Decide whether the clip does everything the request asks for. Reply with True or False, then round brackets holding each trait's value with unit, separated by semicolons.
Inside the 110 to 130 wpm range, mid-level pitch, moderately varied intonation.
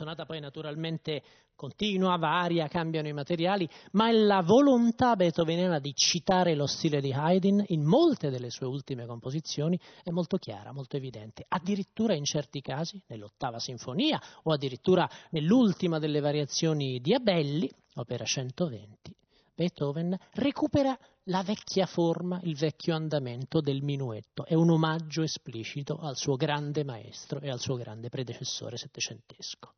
False (140 wpm; 155 Hz; 4.6 semitones)